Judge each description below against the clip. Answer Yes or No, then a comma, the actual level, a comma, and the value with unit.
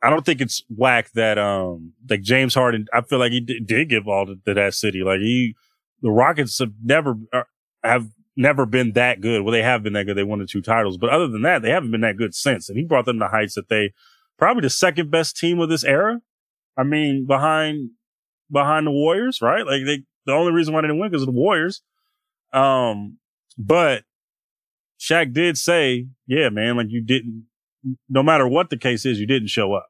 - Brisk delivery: Yes, fast, 225 wpm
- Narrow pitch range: No, average, 4.8 semitones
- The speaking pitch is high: No, low, 125 Hz